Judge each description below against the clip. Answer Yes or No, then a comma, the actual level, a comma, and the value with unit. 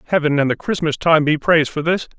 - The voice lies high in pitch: No, medium, 155 Hz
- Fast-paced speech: Yes, fast, 245 wpm